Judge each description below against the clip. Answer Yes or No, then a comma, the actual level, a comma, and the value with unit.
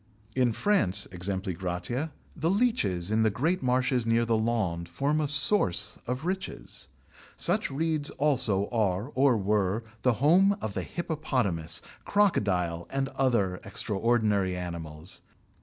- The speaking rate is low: Yes, slow, 125 wpm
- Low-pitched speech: Yes, low, 115 Hz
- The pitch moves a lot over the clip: Yes, wide, 7.1 semitones